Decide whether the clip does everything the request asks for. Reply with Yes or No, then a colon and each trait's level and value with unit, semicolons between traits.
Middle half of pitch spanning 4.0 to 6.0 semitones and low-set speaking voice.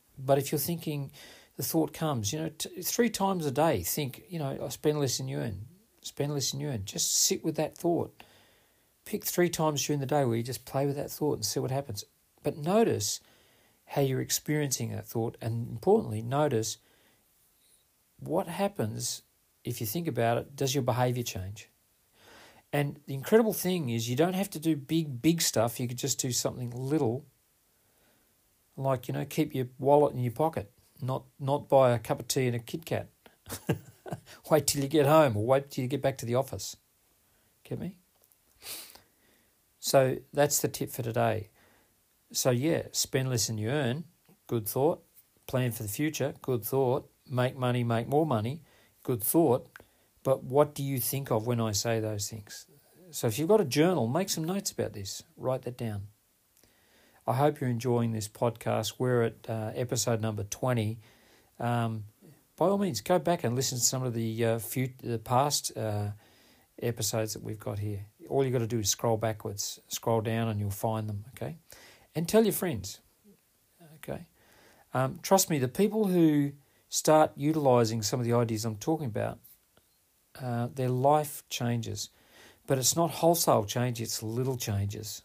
Yes: average, 4.7 semitones; low, 125 Hz